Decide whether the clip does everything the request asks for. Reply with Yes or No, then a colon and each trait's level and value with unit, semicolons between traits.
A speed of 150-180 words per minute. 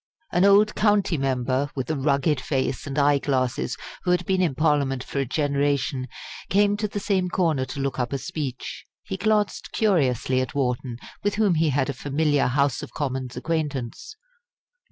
Yes: average, 175 wpm